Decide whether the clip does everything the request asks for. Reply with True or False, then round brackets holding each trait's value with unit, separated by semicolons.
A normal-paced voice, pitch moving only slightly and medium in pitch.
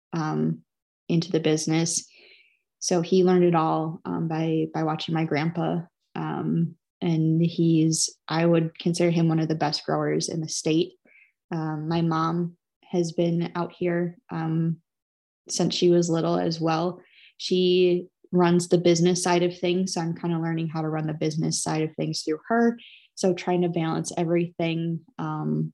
True (170 wpm; 1.7 semitones; 165 Hz)